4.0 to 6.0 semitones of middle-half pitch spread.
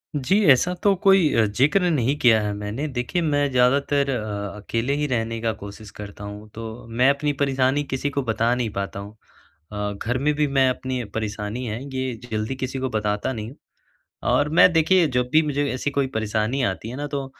Yes: average, 4.5 semitones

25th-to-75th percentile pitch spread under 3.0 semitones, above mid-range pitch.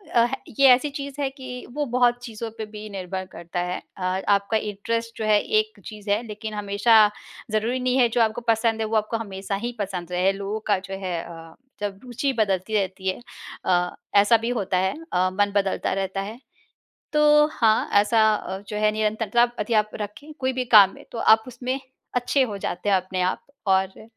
No: average, 3.6 semitones; high, 215 Hz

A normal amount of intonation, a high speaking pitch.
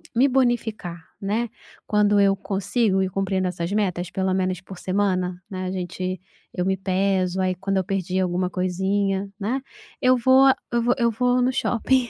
Yes: average, 3.6 semitones; high, 195 Hz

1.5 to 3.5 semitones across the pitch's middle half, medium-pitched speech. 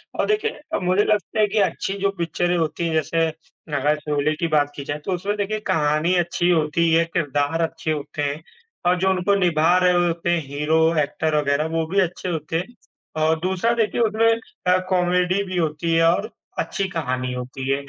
Yes: average, 3.2 semitones; medium, 165 Hz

